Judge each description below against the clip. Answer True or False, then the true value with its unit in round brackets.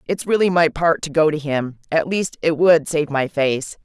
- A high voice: False (155 Hz)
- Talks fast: True (220 wpm)